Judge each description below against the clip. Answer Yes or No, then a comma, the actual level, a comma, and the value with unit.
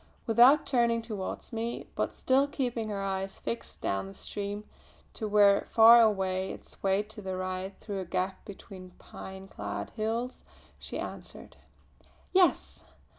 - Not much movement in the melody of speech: No, average, 3.4 semitones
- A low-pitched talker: No, high, 205 Hz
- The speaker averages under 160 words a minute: Yes, average, 145 wpm